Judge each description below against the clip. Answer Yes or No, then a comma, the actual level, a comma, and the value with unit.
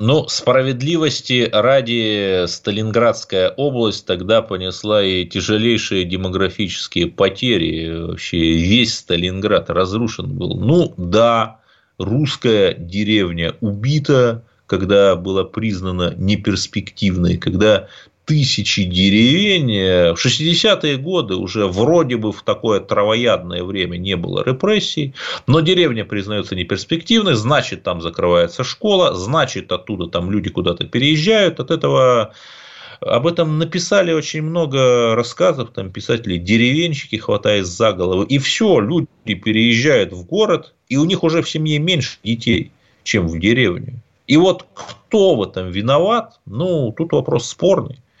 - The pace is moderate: Yes, average, 120 wpm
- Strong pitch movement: Yes, wide, 7.6 semitones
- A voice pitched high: No, low, 115 Hz